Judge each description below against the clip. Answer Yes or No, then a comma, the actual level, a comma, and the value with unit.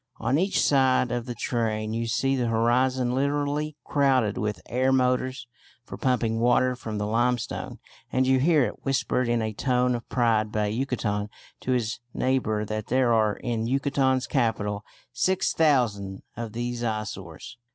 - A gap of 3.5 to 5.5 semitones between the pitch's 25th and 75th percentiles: No, average, 3.0 semitones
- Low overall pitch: Yes, low, 120 Hz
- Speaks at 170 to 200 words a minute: No, average, 160 wpm